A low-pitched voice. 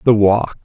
Yes: low, 110 Hz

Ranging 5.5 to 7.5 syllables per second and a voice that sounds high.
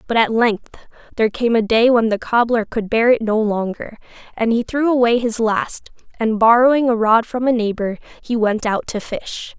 No: 4.9 syllables/s; high, 230 Hz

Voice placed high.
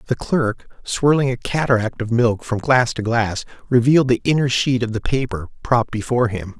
No: low, 120 Hz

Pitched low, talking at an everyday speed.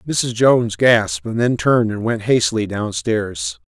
Yes: low, 115 Hz; average, 165 wpm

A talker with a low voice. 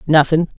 No: medium, 155 Hz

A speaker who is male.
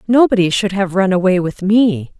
No: female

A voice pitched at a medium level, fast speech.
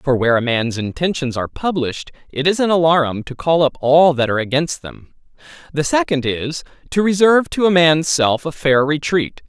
No: medium, 150 Hz; average, 195 wpm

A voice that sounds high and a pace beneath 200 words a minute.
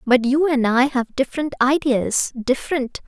Yes: very high, 260 Hz; slow, 135 wpm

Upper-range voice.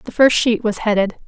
Yes: high, 225 Hz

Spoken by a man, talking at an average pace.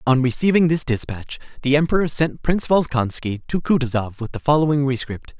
Yes: male; average, 165 wpm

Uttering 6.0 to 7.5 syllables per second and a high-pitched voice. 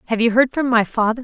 Yes: 6.6 syllables/s; high, 235 Hz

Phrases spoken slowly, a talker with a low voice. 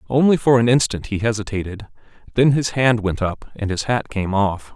No: average, 200 wpm; low, 110 Hz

